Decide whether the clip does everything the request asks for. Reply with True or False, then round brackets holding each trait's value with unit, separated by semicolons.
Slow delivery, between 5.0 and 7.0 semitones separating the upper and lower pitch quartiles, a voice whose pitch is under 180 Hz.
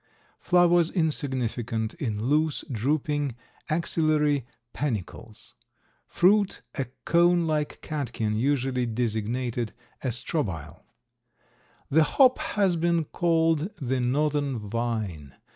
True (95 wpm; 5.6 semitones; 140 Hz)